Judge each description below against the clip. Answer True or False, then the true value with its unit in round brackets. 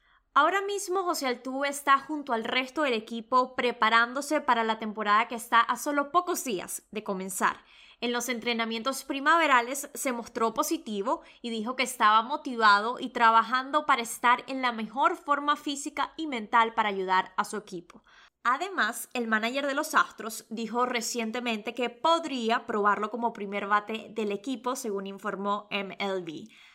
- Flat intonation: False (4.2 semitones)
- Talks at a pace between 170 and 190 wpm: False (155 wpm)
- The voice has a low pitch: False (240 Hz)